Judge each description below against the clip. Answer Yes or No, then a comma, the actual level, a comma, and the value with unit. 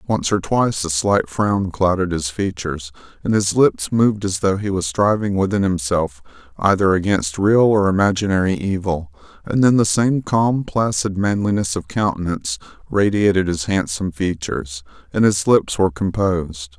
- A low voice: Yes, very low, 95 Hz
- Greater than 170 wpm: No, average, 155 wpm